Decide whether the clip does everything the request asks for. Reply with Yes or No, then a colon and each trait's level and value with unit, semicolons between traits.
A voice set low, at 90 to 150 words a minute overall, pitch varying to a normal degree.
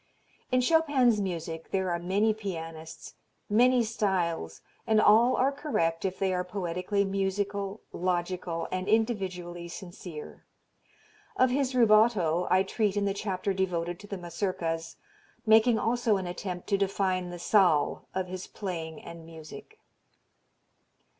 No: high, 190 Hz; slow, 135 wpm; average, 3.7 semitones